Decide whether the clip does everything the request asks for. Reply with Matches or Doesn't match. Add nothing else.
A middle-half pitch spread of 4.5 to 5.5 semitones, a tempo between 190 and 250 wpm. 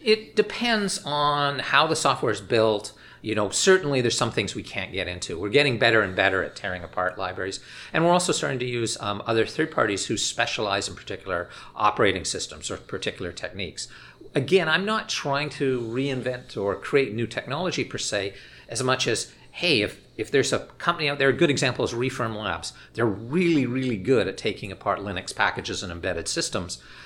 Matches